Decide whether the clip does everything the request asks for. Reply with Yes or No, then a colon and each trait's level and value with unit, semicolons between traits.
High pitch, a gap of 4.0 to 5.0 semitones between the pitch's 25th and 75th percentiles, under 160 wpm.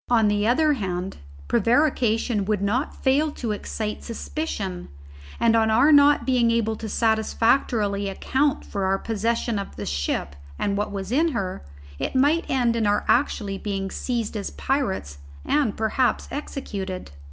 Yes: high, 225 Hz; average, 4.5 semitones; average, 150 wpm